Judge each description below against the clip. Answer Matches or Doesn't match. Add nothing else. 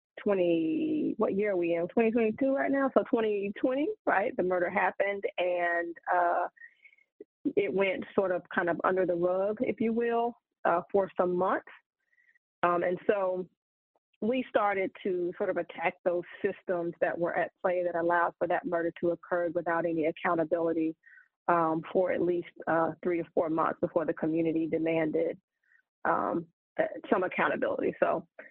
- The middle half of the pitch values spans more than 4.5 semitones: Matches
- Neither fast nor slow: Matches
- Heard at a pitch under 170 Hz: Doesn't match